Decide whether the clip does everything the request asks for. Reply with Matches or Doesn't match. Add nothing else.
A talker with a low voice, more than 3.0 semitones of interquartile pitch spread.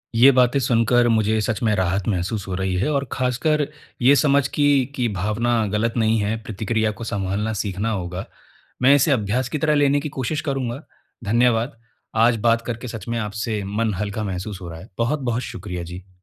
Matches